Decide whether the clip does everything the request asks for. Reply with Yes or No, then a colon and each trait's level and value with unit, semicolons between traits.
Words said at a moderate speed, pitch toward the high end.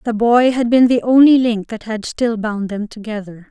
No: fast, 225 wpm; high, 225 Hz